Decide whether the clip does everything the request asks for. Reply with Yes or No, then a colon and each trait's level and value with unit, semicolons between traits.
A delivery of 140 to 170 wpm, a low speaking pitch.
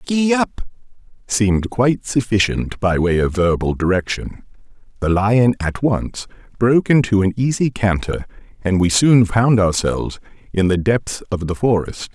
Yes: average, 150 wpm; low, 110 Hz